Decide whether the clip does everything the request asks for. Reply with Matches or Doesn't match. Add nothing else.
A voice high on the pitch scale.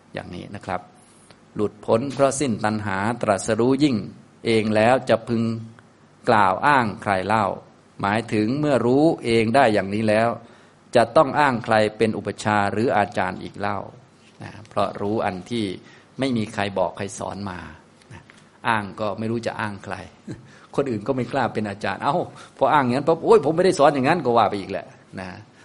Doesn't match